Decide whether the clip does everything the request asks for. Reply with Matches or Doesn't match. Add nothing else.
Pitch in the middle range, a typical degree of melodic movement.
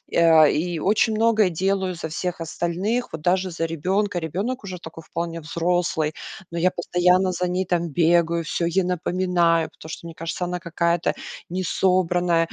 Doesn't match